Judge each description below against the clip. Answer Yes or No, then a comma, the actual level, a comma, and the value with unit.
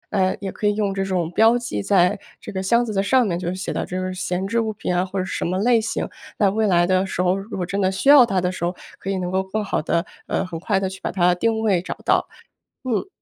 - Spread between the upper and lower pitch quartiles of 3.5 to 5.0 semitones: No, average, 2.7 semitones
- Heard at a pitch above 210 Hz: No, high, 190 Hz